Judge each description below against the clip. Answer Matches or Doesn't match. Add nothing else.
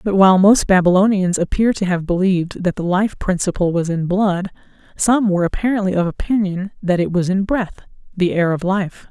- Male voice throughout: Doesn't match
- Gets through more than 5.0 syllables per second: Matches